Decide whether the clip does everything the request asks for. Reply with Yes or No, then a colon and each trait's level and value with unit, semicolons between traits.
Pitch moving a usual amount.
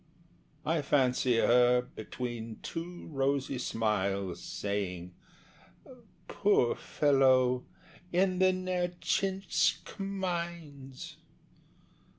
No: wide, 6.6 semitones